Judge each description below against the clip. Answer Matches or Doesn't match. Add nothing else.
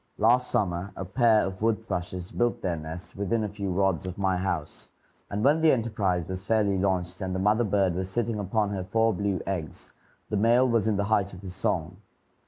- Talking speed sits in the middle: Doesn't match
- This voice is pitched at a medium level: Doesn't match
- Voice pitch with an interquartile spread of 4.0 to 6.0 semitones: Doesn't match